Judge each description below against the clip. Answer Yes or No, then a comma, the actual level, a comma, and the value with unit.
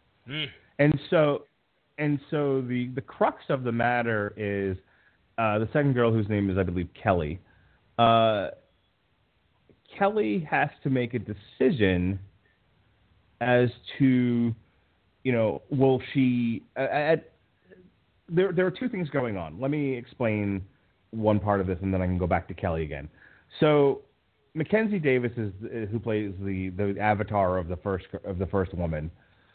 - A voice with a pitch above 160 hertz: No, low, 110 Hz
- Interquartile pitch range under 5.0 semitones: No, wide, 5.4 semitones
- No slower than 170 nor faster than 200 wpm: No, average, 155 wpm